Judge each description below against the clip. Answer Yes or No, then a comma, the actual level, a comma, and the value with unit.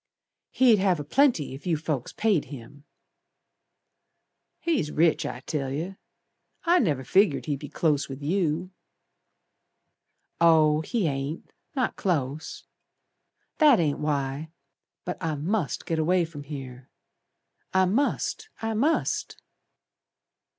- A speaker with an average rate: No, slow, 120 wpm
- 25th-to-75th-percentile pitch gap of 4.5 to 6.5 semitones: Yes, average, 5.1 semitones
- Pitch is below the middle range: No, medium, 160 Hz